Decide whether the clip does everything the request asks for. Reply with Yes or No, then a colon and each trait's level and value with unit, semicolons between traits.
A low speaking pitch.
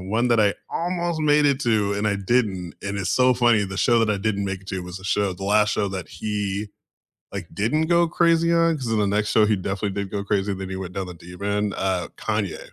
Yes: low, 105 Hz